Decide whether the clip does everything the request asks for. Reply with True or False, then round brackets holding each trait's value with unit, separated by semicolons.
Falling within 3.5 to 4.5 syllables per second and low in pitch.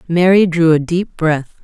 False (4.1 syllables/s; 165 Hz)